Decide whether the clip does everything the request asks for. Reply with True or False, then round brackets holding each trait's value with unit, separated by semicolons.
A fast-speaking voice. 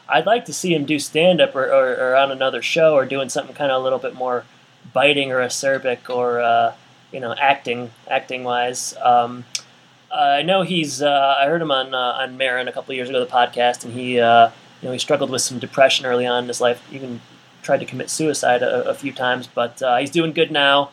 True (230 wpm)